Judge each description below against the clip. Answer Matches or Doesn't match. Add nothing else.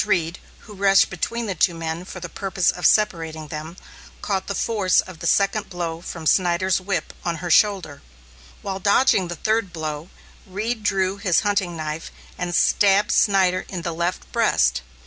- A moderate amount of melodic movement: Matches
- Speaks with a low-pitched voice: Doesn't match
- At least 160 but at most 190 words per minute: Matches